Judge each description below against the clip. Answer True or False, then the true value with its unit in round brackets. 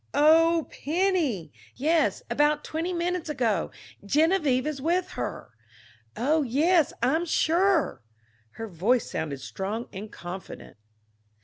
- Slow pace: True (120 wpm)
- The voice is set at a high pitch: True (300 Hz)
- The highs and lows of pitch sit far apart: True (6.7 semitones)